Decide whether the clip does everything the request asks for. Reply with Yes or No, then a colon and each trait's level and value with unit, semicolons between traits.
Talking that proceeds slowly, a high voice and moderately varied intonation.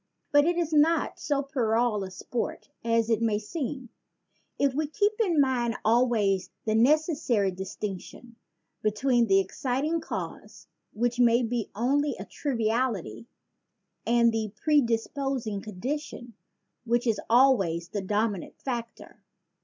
Yes: slow, 130 wpm; high, 235 Hz; average, 4.3 semitones